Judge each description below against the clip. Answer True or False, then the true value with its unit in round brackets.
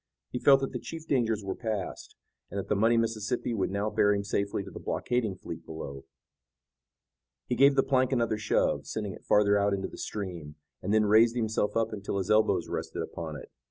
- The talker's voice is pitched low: True (105 Hz)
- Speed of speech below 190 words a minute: False (205 wpm)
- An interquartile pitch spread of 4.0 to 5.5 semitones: False (2.8 semitones)